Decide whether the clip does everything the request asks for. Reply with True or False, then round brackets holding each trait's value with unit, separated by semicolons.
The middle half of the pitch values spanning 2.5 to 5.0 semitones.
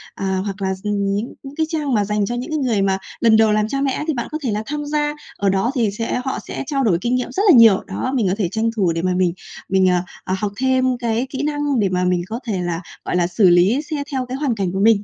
False (5.5 semitones)